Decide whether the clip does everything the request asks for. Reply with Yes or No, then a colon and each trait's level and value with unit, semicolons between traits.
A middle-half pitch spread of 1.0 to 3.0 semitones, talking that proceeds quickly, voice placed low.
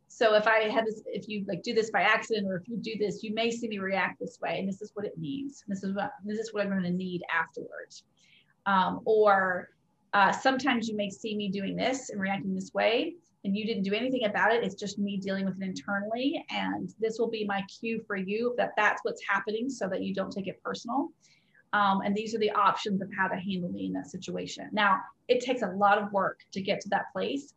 No: narrow, 2.5 semitones; fast, 250 wpm; high, 205 Hz